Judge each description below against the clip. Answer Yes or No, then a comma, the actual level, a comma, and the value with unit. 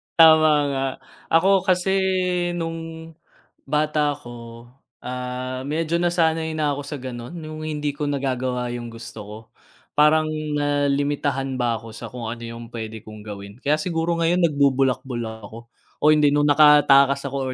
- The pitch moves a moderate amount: Yes, average, 4.3 semitones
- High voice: No, medium, 140 Hz